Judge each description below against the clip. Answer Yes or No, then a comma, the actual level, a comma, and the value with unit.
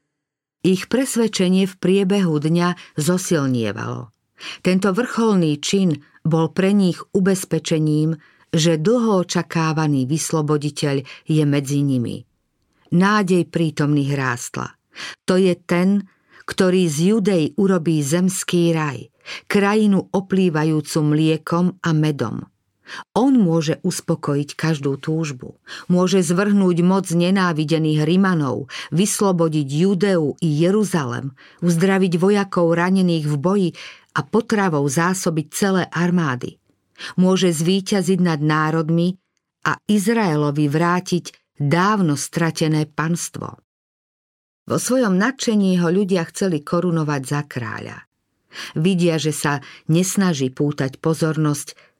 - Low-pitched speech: No, medium, 170 Hz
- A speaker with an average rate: No, slow, 100 wpm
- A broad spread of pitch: No, average, 3.7 semitones